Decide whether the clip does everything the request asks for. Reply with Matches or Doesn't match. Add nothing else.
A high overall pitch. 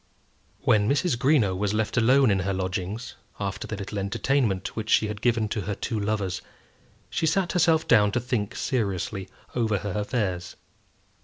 Doesn't match